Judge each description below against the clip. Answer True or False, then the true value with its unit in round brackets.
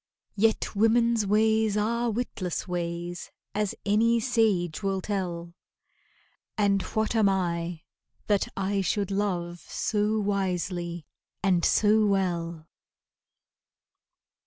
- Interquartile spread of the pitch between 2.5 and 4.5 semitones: True (3.6 semitones)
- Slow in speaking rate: True (100 wpm)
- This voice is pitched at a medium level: False (200 Hz)